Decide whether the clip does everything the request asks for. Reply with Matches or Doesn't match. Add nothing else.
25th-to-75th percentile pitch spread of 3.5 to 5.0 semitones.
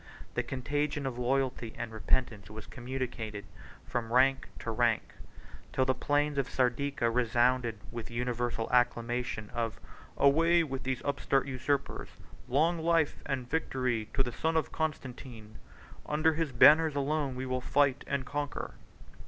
Doesn't match